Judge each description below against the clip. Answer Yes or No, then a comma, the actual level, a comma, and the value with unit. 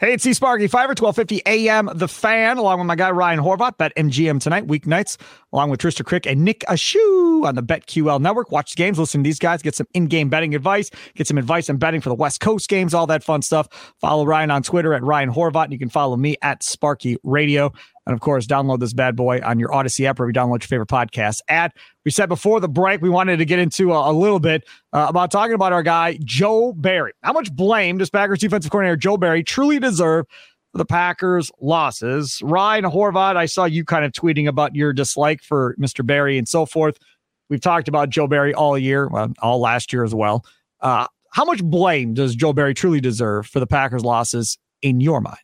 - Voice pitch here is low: No, medium, 160 Hz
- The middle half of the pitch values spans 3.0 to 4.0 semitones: No, average, 4.7 semitones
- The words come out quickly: Yes, fast, 230 wpm